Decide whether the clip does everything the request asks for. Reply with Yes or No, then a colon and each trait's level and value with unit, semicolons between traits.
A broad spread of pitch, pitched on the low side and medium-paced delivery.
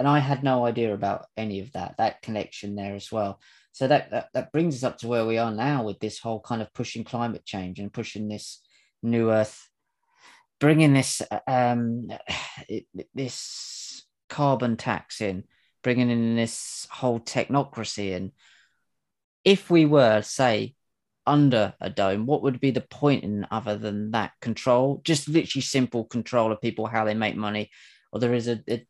No: average, 3.8 semitones; low, 115 Hz; average, 175 wpm